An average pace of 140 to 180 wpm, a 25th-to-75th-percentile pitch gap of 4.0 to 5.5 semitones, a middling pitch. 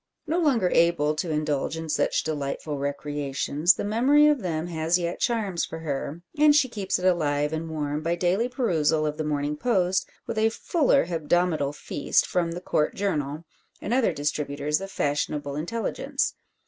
Yes: average, 170 wpm; average, 5.1 semitones; medium, 165 Hz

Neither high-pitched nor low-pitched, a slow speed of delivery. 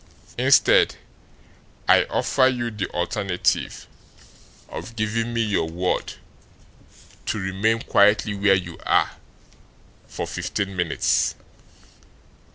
No: low, 100 Hz; slow, 95 wpm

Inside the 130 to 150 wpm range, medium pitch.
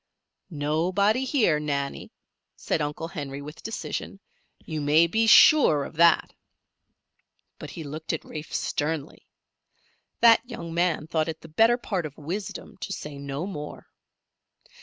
Yes: average, 140 wpm; medium, 160 Hz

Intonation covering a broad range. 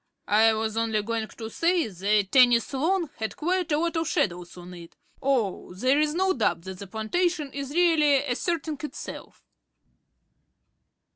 Yes: wide, 6.9 semitones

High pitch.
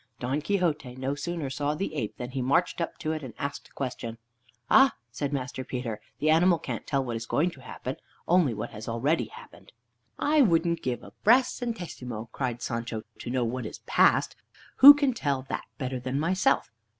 No: medium, 140 Hz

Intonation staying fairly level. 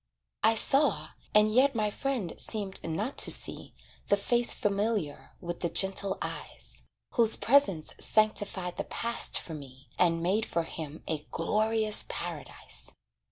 No: average, 4.9 semitones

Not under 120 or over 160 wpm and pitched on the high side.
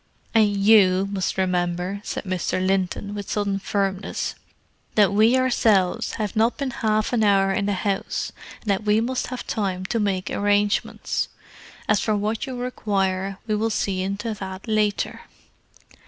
Yes: average, 155 wpm; high, 205 Hz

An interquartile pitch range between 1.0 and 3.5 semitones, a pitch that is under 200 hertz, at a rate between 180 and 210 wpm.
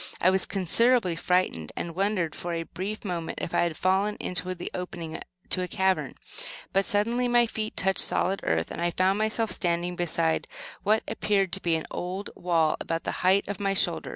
Yes: average, 2.8 semitones; medium, 185 Hz; average, 195 wpm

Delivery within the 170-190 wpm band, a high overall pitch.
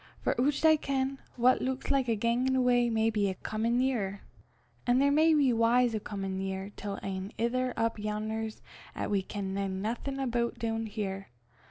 Yes: average, 180 wpm; high, 230 Hz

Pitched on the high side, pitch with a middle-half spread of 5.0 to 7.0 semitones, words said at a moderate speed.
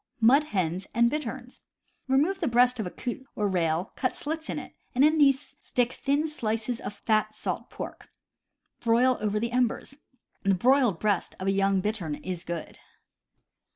Yes: high, 235 Hz; average, 5.3 semitones; average, 175 wpm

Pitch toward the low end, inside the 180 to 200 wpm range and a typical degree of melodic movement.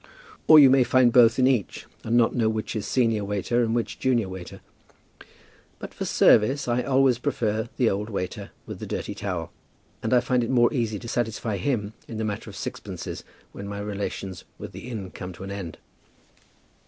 Yes: low, 115 Hz; average, 195 wpm; average, 3.3 semitones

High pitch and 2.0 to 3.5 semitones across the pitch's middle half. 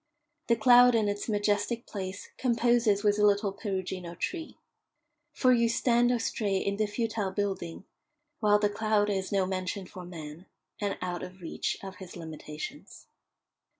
Yes: high, 205 Hz; average, 3.2 semitones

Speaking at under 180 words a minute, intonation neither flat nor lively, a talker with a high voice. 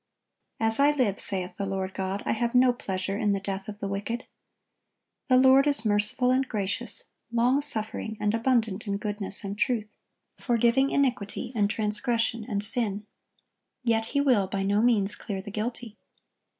Yes: average, 165 wpm; average, 3.3 semitones; high, 215 Hz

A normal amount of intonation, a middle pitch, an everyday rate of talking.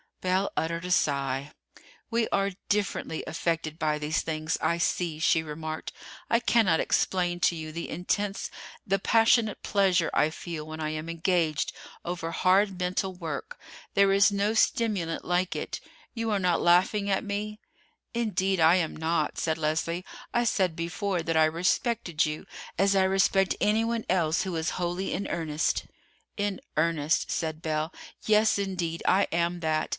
Yes: average, 3.6 semitones; medium, 175 Hz; average, 160 wpm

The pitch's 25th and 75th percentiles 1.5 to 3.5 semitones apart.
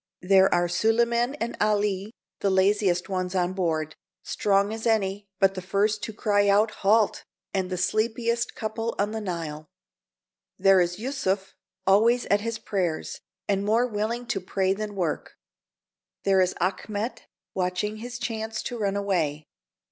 Yes: average, 2.8 semitones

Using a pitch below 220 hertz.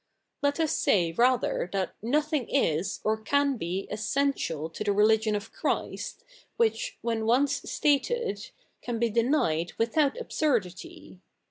No: high, 235 Hz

